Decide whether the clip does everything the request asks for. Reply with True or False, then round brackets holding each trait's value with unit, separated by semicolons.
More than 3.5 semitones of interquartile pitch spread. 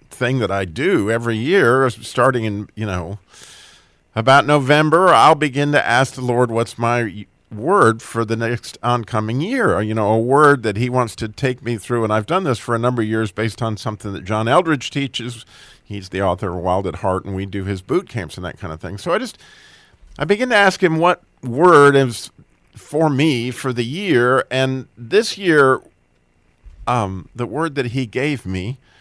True (4.2 semitones)